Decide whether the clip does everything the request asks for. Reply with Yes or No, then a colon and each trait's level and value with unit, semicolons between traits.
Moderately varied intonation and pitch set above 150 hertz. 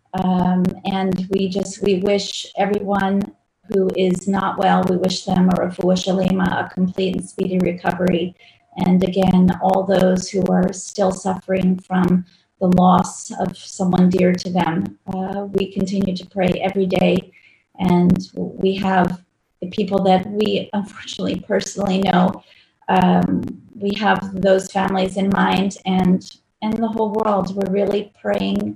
No: narrow, 1.1 semitones; high, 190 Hz